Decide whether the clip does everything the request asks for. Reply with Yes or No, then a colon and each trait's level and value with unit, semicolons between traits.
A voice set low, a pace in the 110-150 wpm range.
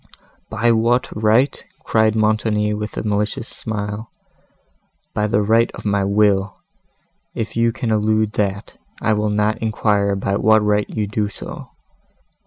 Yes: low, 105 Hz; average, 145 wpm